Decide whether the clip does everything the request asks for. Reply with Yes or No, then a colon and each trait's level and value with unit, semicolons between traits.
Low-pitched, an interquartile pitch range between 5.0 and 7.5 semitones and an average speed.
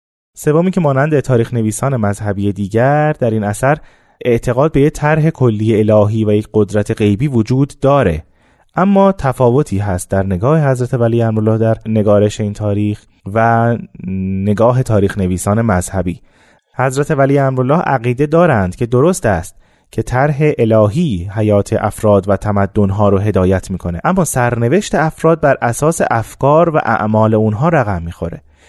Yes: low, 115 Hz; wide, 5.4 semitones; average, 145 wpm